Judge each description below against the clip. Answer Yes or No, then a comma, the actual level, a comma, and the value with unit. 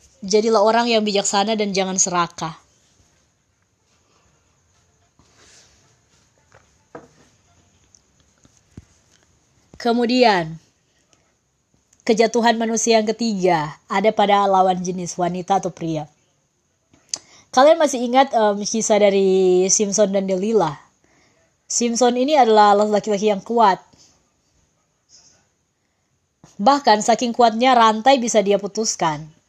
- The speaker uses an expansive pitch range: No, average, 4.1 semitones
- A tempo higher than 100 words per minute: No, slow, 85 wpm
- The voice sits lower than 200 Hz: No, high, 205 Hz